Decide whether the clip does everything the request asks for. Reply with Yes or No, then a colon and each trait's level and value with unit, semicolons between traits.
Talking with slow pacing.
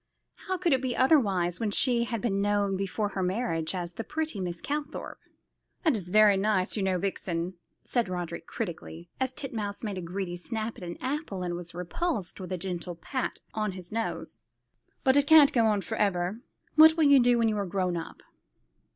No: average, 195 wpm